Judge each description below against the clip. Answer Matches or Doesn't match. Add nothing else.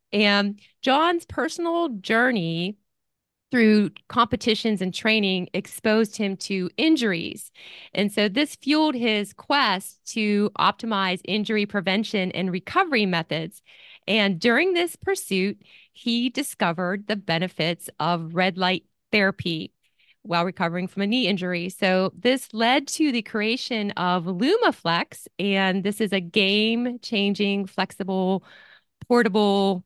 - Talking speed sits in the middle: Doesn't match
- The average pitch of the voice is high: Matches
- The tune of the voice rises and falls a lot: Doesn't match